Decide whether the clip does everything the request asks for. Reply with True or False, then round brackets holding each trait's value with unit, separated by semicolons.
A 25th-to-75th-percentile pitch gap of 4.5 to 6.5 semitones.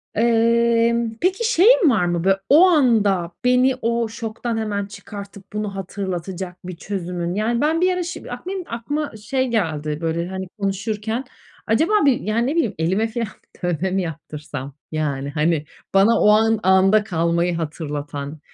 True (5.2 semitones)